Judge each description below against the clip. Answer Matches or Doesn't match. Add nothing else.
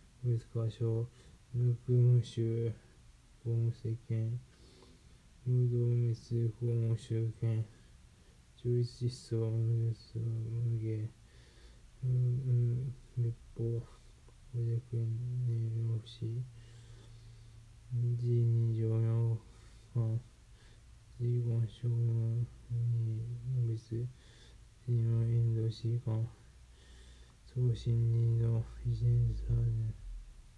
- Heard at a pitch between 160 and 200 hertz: Doesn't match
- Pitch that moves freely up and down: Doesn't match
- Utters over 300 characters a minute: Doesn't match